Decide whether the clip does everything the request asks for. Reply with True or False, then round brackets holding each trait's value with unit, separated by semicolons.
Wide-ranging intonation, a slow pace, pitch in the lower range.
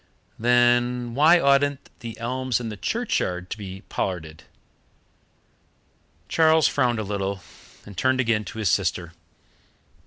False (5.0 semitones; 125 wpm; 120 Hz)